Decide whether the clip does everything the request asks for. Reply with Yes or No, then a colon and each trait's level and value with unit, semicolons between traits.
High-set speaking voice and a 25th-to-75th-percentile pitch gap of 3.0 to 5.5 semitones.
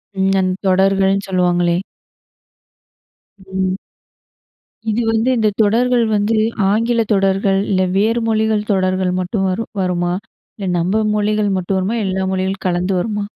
No: high, 195 Hz; narrow, 2.5 semitones